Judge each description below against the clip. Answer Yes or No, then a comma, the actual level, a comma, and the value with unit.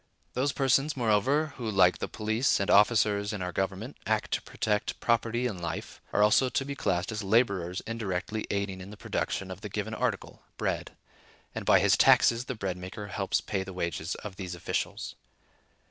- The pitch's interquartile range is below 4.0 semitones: Yes, average, 3.6 semitones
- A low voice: Yes, low, 105 Hz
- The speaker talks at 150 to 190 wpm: Yes, average, 185 wpm